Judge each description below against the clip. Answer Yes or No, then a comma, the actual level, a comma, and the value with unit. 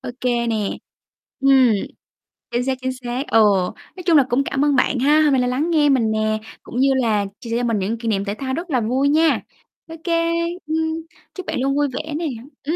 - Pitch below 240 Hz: No, very high, 260 Hz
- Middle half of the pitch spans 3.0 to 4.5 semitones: Yes, average, 4.1 semitones